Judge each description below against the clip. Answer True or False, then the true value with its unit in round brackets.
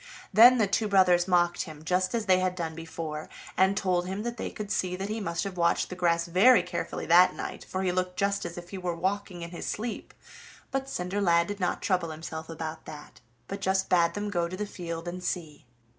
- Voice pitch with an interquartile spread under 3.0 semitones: True (2.6 semitones)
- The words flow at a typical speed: False (225 wpm)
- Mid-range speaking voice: True (180 Hz)